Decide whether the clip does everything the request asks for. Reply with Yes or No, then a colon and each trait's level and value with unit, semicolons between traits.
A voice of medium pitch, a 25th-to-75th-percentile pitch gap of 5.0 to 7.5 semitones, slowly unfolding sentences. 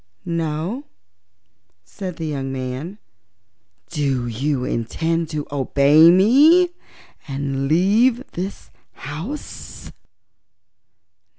Yes: medium, 155 Hz; wide, 5.6 semitones; slow, 80 wpm